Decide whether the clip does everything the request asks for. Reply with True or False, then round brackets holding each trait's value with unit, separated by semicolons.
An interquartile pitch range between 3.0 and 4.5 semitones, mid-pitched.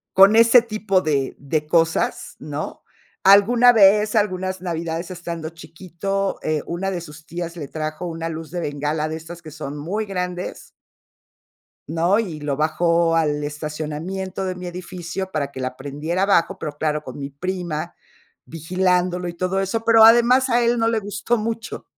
True (3.8 semitones; 175 Hz)